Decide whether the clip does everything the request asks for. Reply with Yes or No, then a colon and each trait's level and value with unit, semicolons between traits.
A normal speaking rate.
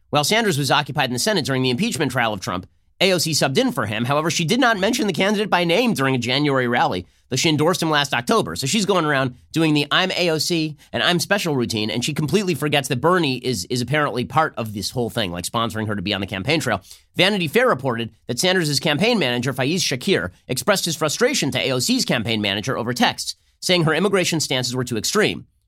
No: fast, 225 wpm